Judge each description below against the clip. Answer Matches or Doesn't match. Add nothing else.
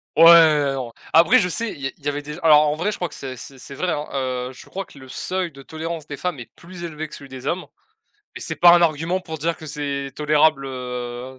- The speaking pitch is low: Doesn't match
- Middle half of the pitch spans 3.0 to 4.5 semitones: Matches